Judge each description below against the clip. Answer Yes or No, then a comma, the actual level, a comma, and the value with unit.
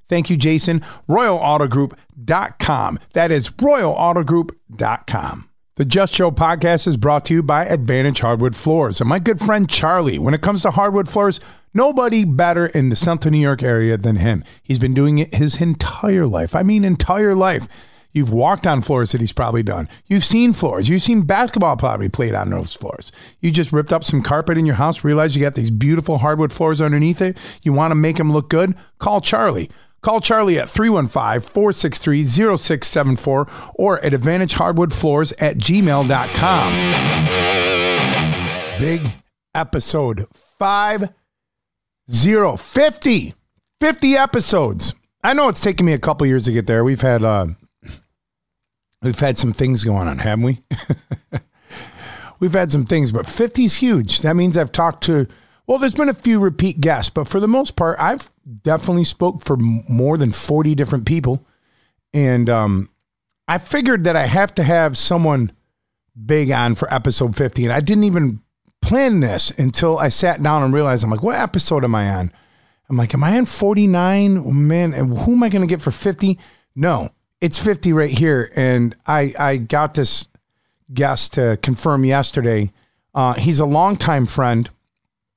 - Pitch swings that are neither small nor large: No, wide, 6.0 semitones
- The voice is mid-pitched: Yes, medium, 150 Hz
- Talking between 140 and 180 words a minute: Yes, average, 165 wpm